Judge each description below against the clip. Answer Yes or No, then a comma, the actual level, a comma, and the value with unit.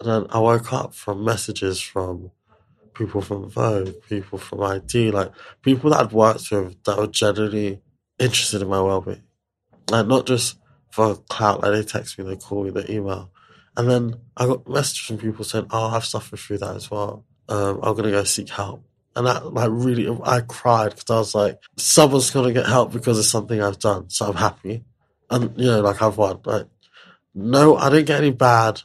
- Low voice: Yes, low, 110 Hz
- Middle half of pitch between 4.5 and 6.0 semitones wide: No, average, 3.2 semitones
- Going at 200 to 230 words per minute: Yes, fast, 205 wpm